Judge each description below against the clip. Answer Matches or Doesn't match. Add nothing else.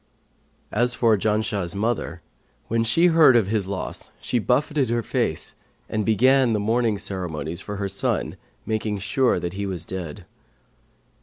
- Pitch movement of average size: Matches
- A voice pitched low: Matches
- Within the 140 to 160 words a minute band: Matches